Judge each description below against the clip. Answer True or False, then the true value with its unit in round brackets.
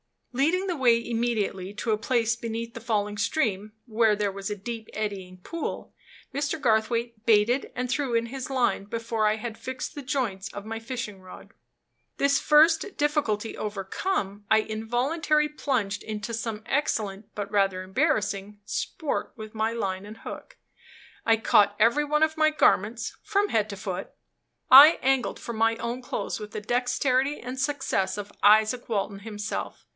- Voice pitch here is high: True (225 Hz)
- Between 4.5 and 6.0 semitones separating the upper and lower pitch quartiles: False (3.9 semitones)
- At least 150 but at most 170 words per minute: True (160 wpm)